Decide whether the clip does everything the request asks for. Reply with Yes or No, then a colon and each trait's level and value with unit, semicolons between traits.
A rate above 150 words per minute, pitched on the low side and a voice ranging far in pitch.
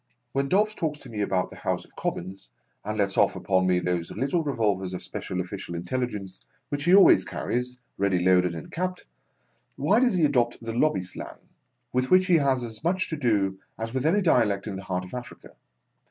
Yes: average, 200 wpm; low, 115 Hz; wide, 7.5 semitones